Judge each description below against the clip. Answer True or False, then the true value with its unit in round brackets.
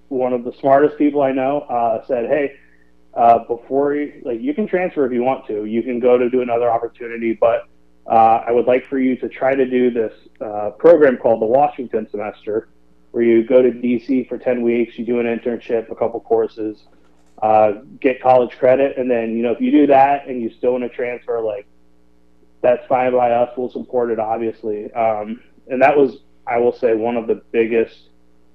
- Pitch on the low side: True (120 Hz)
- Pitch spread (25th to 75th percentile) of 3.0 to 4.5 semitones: False (2.4 semitones)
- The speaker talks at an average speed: False (210 wpm)